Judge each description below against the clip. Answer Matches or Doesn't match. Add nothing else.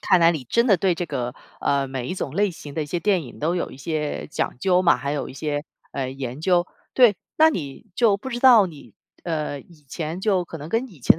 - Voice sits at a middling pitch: Matches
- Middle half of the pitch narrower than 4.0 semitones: Doesn't match